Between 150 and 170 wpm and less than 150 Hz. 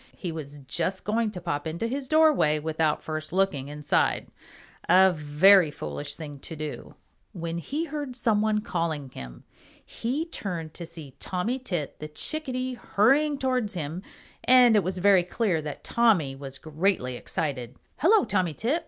No: average, 160 wpm; medium, 180 Hz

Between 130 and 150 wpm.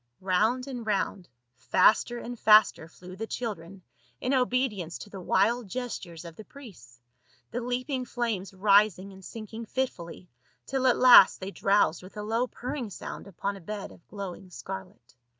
No: average, 160 wpm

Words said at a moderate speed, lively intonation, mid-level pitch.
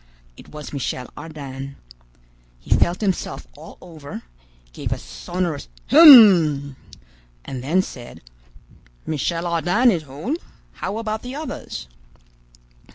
No: slow, 110 wpm; wide, 6.8 semitones; medium, 165 Hz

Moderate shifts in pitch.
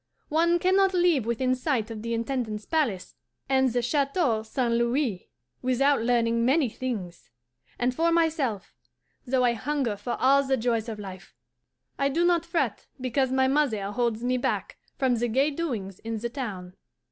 Yes: average, 3.6 semitones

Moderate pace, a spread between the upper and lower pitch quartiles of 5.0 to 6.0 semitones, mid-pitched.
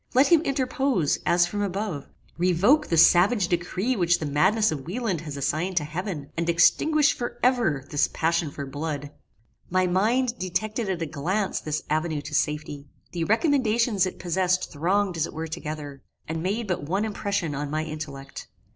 Yes: average, 175 wpm; wide, 5.5 semitones; medium, 175 Hz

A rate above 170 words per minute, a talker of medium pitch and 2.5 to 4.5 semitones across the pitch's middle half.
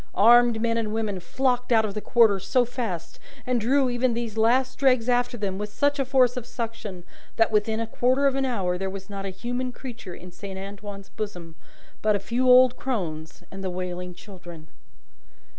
No: average, 195 wpm; high, 225 Hz; average, 4.2 semitones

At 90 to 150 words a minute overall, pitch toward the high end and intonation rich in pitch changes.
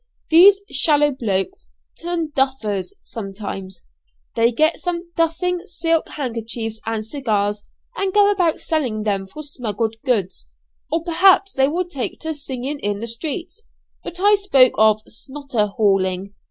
Yes: average, 140 wpm; very high, 265 Hz; wide, 7.5 semitones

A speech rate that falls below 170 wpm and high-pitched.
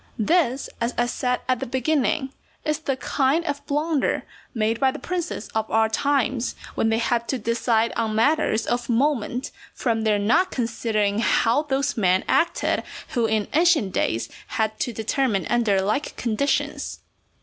Yes: average, 160 wpm; high, 240 Hz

